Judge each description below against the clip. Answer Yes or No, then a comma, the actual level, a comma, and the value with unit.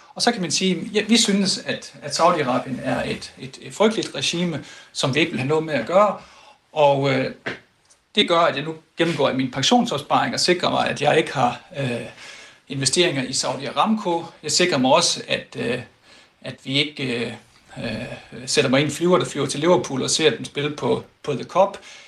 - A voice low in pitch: No, medium, 155 Hz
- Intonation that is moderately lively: Yes, average, 4.7 semitones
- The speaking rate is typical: Yes, average, 200 wpm